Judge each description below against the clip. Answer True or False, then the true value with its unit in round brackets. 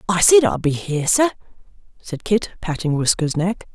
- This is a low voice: False (185 Hz)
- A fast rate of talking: False (175 wpm)